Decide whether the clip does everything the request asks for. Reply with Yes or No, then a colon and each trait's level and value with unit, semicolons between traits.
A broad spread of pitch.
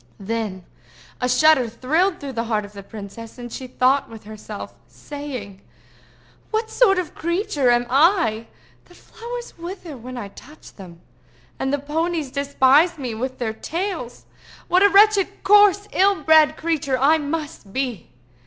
Yes: wide, 6.7 semitones